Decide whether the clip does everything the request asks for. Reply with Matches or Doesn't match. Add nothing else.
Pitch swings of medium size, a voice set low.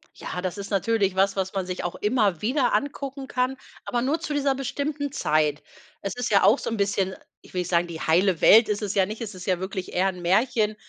Doesn't match